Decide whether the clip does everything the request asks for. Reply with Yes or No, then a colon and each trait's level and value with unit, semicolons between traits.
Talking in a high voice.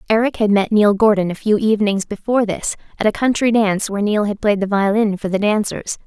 Yes: high, 210 Hz